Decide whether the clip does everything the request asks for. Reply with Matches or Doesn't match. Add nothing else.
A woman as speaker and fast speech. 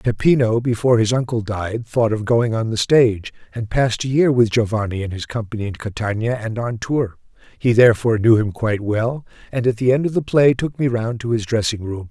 Doesn't match